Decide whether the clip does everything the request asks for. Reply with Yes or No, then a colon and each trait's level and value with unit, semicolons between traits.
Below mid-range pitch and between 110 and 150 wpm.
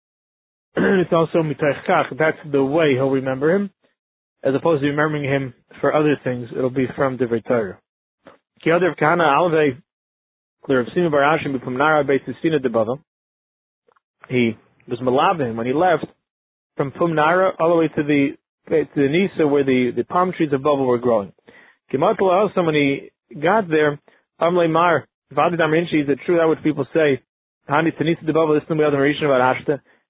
No: medium, 150 Hz; average, 140 wpm